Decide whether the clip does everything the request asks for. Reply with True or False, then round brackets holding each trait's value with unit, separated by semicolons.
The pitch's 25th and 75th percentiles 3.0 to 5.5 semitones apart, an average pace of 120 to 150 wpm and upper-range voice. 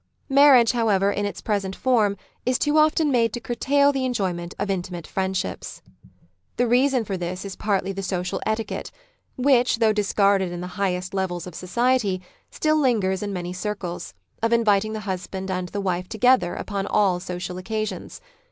False (4.5 semitones; 180 wpm; 200 Hz)